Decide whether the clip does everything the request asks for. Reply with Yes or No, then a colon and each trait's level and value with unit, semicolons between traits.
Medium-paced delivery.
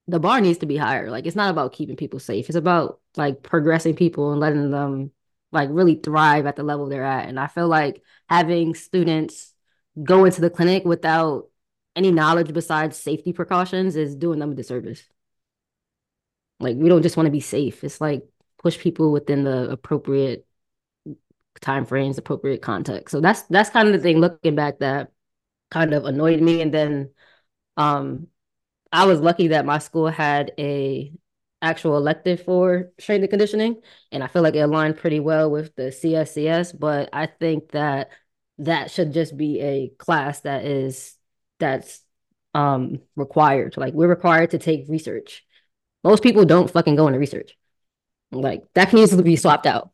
Yes: average, 175 wpm